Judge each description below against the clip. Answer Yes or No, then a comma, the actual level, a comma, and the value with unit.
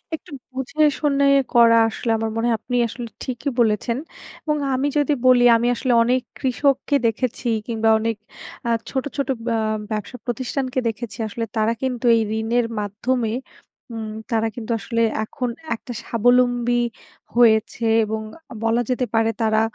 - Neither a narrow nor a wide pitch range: No, narrow, 2.3 semitones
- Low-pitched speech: No, high, 240 Hz